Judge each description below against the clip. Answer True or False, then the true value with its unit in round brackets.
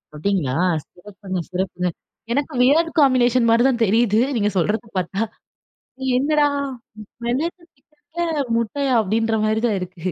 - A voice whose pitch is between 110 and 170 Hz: False (230 Hz)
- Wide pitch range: True (6.0 semitones)